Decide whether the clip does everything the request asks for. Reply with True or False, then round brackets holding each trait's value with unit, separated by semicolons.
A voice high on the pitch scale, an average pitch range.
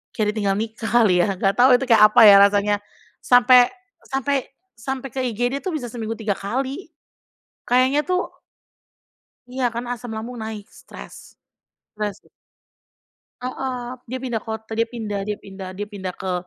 True (230 Hz; 3.4 semitones)